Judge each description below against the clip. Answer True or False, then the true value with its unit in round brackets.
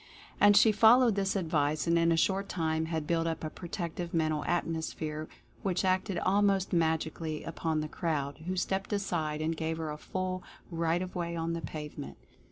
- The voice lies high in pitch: False (165 Hz)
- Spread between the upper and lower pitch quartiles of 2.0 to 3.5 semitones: True (2.8 semitones)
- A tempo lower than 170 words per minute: False (185 wpm)